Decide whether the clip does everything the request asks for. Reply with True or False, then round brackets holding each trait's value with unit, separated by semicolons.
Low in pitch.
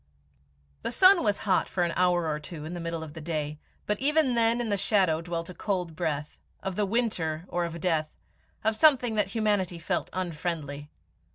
False (180 Hz)